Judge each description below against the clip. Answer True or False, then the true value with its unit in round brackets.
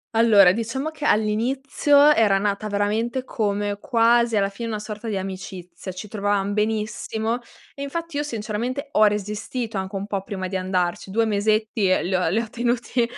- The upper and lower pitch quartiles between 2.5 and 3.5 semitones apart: True (2.8 semitones)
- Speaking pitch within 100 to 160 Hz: False (215 Hz)